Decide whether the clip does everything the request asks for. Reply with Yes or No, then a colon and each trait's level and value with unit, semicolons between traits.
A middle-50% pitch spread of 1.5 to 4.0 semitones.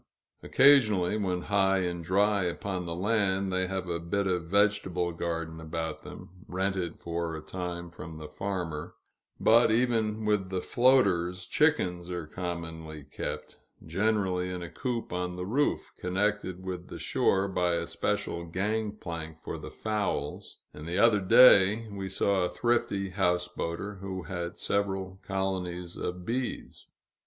Yes: average, 2.8 semitones